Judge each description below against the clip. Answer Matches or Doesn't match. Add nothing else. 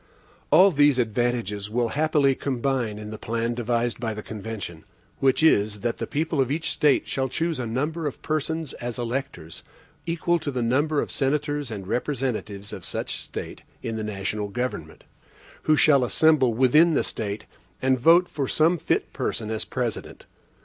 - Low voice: Matches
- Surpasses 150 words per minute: Matches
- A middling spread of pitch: Matches